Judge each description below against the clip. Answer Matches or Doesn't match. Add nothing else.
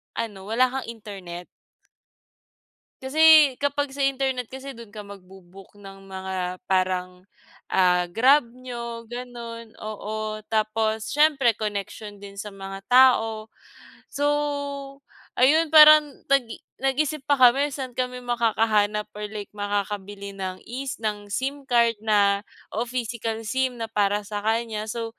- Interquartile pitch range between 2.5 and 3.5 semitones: Doesn't match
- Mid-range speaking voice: Doesn't match